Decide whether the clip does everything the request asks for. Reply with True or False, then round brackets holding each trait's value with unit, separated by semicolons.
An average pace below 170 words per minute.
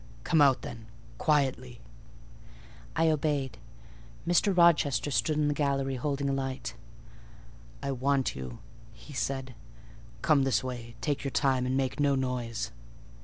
True (135 wpm)